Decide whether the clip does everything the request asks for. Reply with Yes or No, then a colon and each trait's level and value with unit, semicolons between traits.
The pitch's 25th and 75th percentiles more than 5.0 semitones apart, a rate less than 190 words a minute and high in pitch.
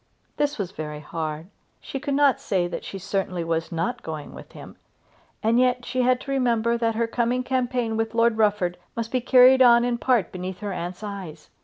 No: wide, 5.5 semitones; average, 200 wpm; high, 225 Hz